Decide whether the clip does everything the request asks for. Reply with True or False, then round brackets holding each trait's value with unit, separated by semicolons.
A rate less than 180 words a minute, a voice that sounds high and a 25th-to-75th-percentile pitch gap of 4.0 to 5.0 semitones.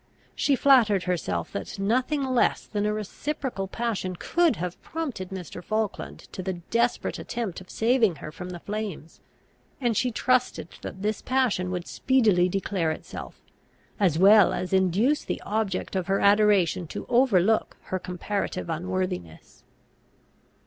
True (140 wpm; 200 Hz; 4.5 semitones)